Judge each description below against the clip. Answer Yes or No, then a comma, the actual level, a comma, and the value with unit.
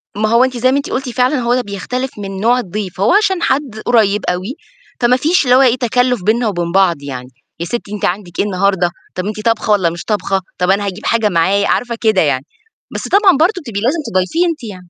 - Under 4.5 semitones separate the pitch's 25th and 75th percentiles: No, average, 4.8 semitones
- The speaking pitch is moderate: No, high, 215 Hz